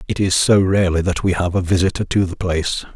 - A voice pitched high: No, very low, 90 Hz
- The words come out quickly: Yes, fast, 245 wpm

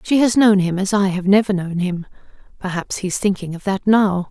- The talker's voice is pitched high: Yes, high, 195 Hz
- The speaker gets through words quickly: Yes, fast, 225 wpm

